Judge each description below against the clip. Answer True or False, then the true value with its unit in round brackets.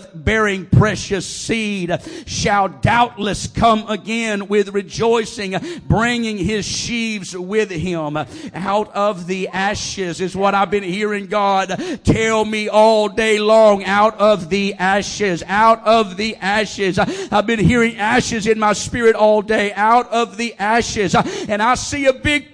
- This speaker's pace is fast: False (145 wpm)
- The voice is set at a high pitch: True (210 Hz)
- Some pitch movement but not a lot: False (2.3 semitones)